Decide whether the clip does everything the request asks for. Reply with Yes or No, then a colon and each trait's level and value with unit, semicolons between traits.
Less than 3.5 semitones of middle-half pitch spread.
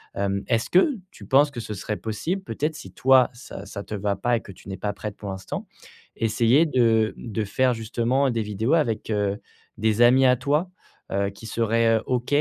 No: average, 3.8 semitones